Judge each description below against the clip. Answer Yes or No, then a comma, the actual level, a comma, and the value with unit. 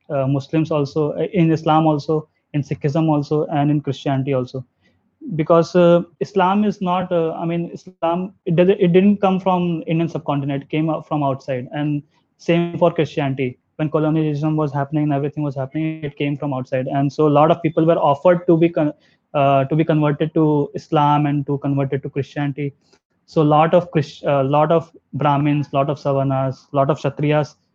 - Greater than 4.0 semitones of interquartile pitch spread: No, average, 2.7 semitones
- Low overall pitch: No, medium, 150 Hz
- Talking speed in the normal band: Yes, average, 185 wpm